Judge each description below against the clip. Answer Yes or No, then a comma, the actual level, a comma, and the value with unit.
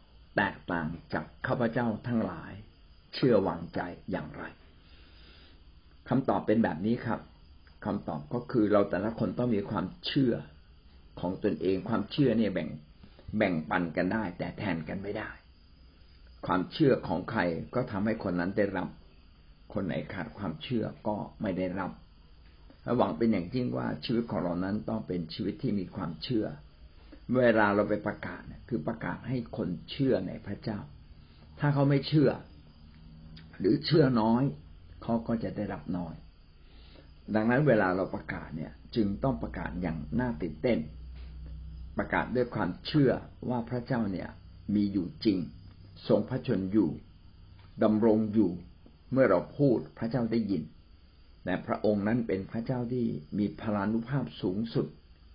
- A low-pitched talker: Yes, very low, 90 Hz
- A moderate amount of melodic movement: No, wide, 6.1 semitones